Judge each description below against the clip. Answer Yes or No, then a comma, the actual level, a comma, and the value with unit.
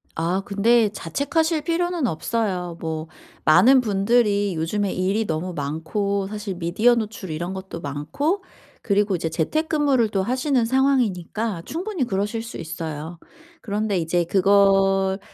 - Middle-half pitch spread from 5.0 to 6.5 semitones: Yes, wide, 5.4 semitones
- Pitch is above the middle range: Yes, high, 200 Hz